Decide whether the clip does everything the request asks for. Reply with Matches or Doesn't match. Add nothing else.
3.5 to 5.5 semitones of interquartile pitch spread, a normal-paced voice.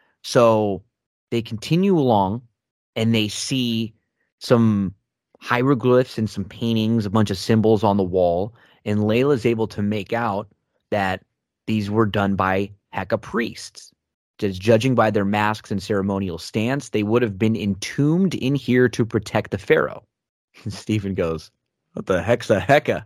Doesn't match